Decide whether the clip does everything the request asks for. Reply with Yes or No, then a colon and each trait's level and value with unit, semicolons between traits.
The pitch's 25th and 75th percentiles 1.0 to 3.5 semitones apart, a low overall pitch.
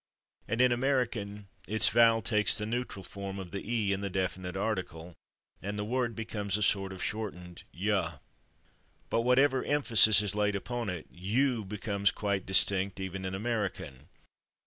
Yes: average, 3.2 semitones; low, 100 Hz